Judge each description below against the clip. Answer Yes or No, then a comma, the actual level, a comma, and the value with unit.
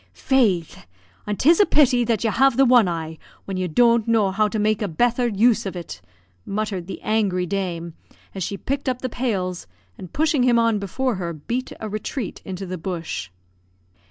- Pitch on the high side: Yes, high, 210 Hz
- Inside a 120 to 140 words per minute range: No, average, 190 wpm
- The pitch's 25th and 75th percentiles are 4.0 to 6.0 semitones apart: Yes, average, 4.9 semitones